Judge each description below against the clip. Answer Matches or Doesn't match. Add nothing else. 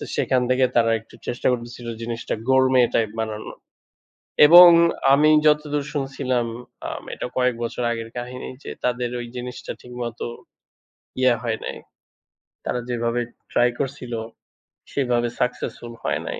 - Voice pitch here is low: Matches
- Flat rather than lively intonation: Matches